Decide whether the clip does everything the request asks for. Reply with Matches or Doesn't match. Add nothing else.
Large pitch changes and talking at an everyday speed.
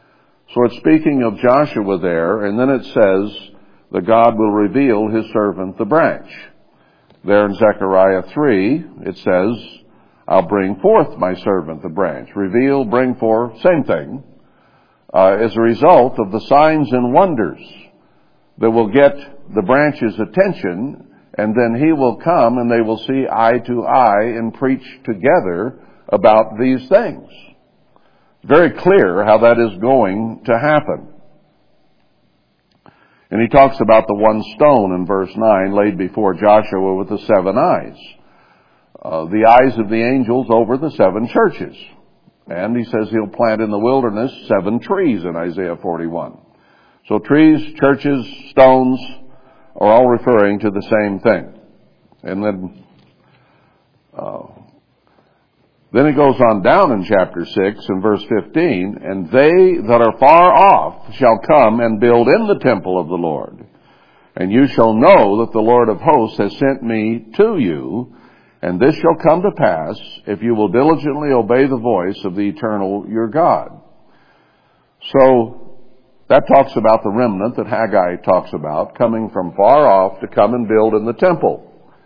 Doesn't match